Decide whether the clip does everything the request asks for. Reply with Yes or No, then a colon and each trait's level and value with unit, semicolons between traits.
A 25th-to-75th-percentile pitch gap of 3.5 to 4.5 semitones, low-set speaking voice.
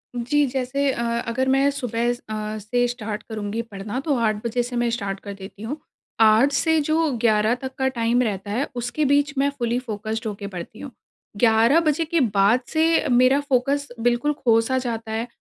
No: average, 3.8 semitones; high, 240 Hz